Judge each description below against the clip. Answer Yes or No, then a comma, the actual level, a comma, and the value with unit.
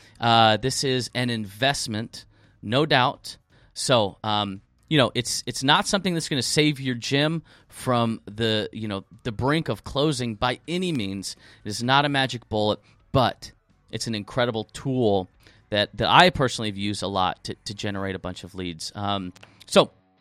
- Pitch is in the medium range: No, low, 110 Hz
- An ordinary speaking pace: Yes, average, 175 wpm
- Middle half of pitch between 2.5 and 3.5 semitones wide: No, average, 4.2 semitones